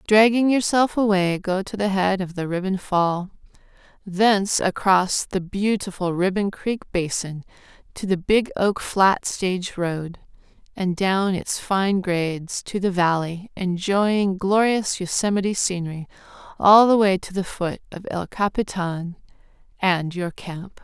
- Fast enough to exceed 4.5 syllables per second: No, 4.1 syllables/s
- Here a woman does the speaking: Yes, female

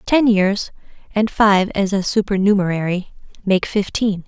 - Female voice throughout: Yes, female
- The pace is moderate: No, slow, 125 wpm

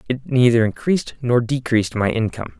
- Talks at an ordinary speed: Yes, average, 160 wpm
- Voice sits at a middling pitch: No, low, 120 Hz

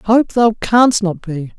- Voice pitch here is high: Yes, high, 210 Hz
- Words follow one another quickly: No, average, 190 wpm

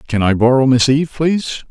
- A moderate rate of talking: No, fast, 210 wpm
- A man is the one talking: Yes, male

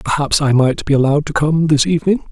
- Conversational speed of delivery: No, fast, 235 wpm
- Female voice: No, male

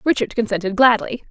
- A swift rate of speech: No, average, 140 wpm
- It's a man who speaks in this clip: No, female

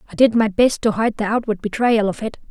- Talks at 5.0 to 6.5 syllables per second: Yes, 6.1 syllables/s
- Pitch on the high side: Yes, high, 215 Hz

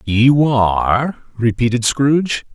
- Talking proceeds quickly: No, slow, 95 wpm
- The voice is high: No, low, 125 Hz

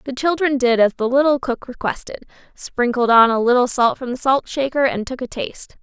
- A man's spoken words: No, female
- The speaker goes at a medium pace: No, fast, 215 wpm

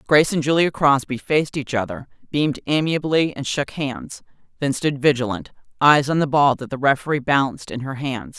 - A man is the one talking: No, female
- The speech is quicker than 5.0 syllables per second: Yes, 5.5 syllables/s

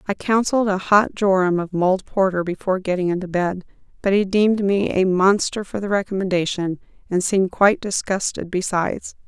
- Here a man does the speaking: No, female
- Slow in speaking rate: No, average, 170 wpm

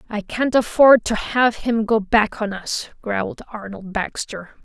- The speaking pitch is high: Yes, high, 220 Hz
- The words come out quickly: No, average, 170 wpm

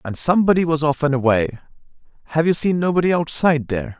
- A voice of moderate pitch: Yes, medium, 150 Hz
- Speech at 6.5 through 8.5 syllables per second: Yes, 6.9 syllables/s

